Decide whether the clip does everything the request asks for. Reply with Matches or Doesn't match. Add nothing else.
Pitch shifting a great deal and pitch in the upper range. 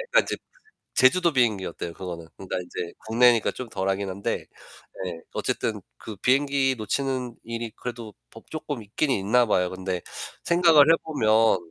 Doesn't match